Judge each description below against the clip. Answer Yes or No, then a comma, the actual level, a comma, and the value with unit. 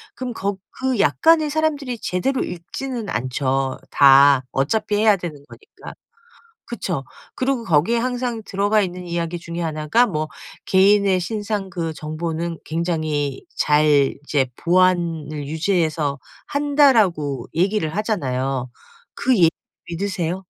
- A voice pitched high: No, medium, 175 Hz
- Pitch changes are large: Yes, wide, 6.0 semitones